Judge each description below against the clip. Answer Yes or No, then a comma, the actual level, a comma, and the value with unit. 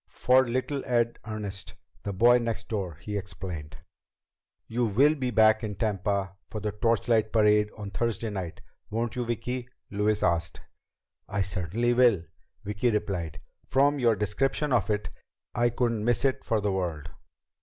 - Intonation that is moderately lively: Yes, average, 3.3 semitones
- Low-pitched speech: Yes, low, 110 Hz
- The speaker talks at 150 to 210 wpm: Yes, average, 155 wpm